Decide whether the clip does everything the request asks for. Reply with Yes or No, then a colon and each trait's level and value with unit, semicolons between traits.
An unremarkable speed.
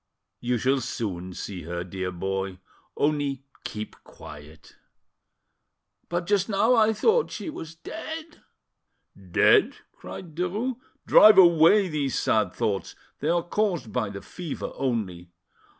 No: slow, 125 wpm